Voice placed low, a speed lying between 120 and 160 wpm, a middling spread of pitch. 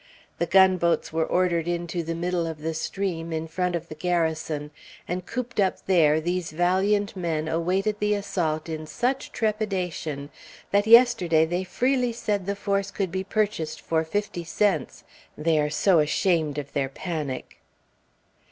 No: medium, 175 Hz; average, 155 wpm; average, 3.8 semitones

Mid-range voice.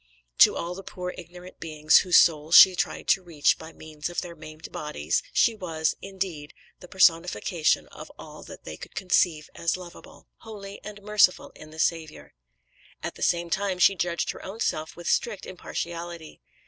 Yes: medium, 175 Hz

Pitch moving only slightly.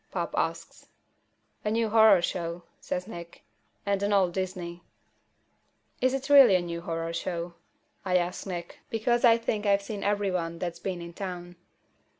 No: average, 3.2 semitones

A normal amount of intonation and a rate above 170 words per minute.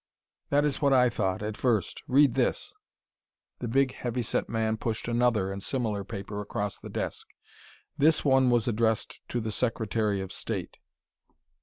No: average, 3.4 semitones; average, 165 wpm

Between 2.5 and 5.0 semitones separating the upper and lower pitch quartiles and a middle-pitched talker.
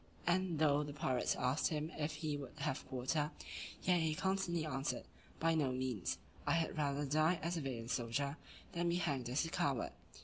Yes: average, 3.5 semitones; medium, 150 Hz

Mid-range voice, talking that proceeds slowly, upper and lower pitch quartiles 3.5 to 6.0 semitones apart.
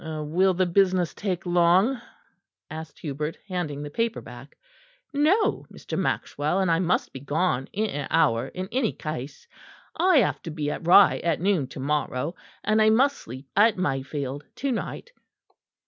No: medium, 170 Hz; average, 160 wpm; wide, 5.6 semitones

